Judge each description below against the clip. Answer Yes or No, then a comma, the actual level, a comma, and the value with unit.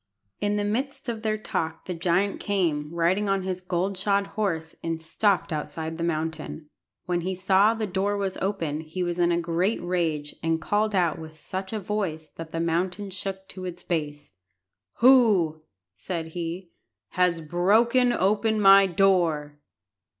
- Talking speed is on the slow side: No, average, 165 wpm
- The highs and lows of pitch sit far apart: No, average, 3.6 semitones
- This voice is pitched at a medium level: Yes, medium, 180 Hz